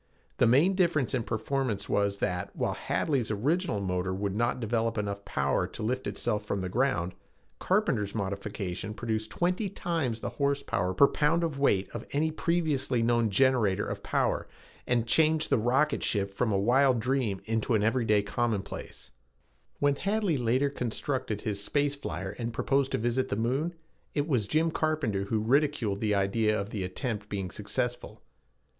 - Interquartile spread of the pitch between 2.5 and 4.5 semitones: No, wide, 5.5 semitones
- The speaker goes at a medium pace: Yes, average, 165 wpm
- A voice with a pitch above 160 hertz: No, low, 115 Hz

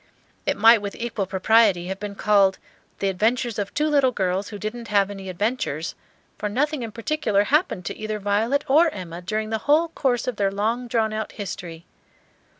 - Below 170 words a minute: No, average, 185 wpm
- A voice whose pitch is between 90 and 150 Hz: No, high, 215 Hz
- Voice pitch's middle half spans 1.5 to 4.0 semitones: Yes, average, 3.5 semitones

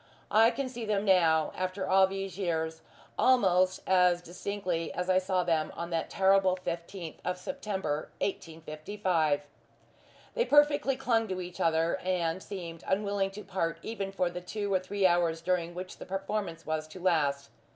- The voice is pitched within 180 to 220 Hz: Yes, medium, 185 Hz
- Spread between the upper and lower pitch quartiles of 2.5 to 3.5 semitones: Yes, average, 2.9 semitones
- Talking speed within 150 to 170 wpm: Yes, average, 160 wpm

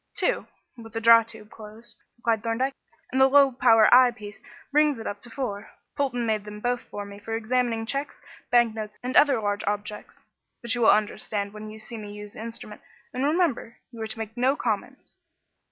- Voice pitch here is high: Yes, high, 225 Hz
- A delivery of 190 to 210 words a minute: Yes, average, 200 wpm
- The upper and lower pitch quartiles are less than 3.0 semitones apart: Yes, narrow, 2.6 semitones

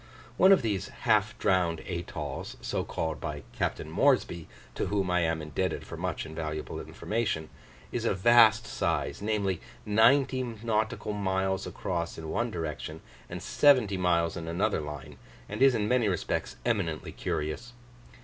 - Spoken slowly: No, average, 150 wpm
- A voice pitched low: Yes, very low, 95 Hz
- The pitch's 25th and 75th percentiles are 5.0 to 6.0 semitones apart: Yes, average, 5.3 semitones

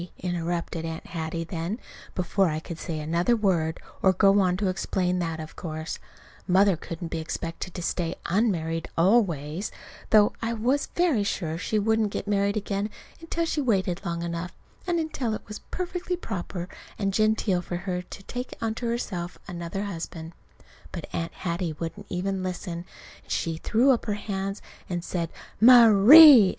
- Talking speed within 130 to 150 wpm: No, average, 165 wpm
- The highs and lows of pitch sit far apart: No, average, 4.2 semitones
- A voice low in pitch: No, medium, 185 Hz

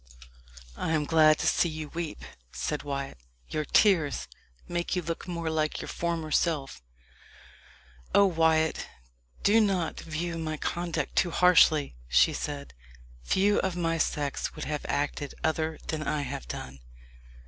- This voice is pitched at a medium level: Yes, medium, 160 Hz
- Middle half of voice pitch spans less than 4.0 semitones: Yes, narrow, 2.4 semitones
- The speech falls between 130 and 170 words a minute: Yes, average, 145 wpm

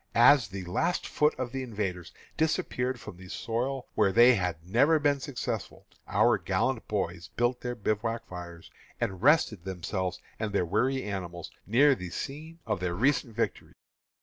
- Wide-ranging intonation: Yes, wide, 5.9 semitones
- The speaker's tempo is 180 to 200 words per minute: No, average, 160 wpm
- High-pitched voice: No, low, 115 Hz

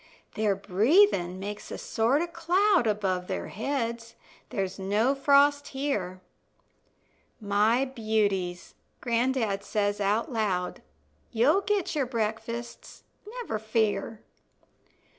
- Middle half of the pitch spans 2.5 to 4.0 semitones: No, average, 5.1 semitones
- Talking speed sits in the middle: No, slow, 105 wpm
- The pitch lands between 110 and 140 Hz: No, high, 225 Hz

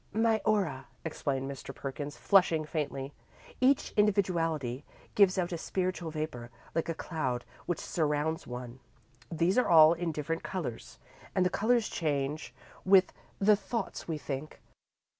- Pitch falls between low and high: Yes, medium, 165 Hz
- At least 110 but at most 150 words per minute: Yes, average, 140 wpm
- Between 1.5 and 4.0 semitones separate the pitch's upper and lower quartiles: No, average, 4.6 semitones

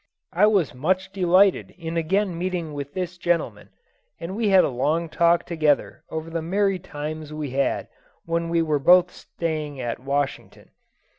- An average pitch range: Yes, average, 3.3 semitones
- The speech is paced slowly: No, average, 160 wpm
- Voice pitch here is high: No, medium, 165 Hz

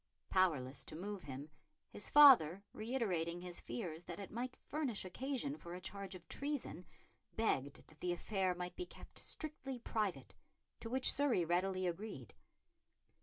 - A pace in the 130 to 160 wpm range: Yes, average, 150 wpm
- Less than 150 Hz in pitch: No, high, 190 Hz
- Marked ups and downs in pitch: Yes, wide, 5.9 semitones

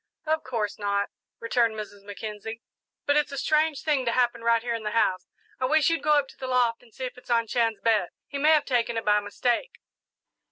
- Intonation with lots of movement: No, average, 3.9 semitones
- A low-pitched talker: No, high, 235 Hz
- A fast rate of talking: Yes, fast, 230 wpm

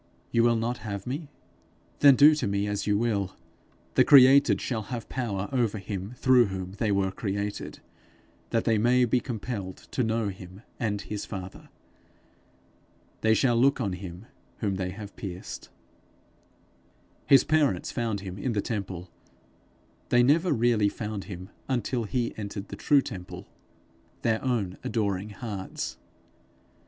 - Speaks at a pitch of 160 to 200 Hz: No, low, 110 Hz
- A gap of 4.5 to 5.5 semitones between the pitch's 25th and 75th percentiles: No, average, 3.7 semitones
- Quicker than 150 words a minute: No, average, 145 wpm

